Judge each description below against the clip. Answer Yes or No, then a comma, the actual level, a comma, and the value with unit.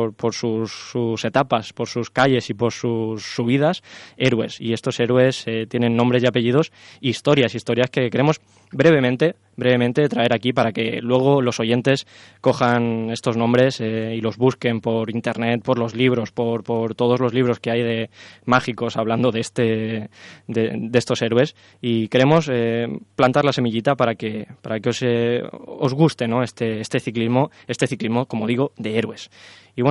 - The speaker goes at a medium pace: Yes, average, 175 wpm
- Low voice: Yes, low, 120 Hz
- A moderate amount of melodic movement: No, narrow, 1.9 semitones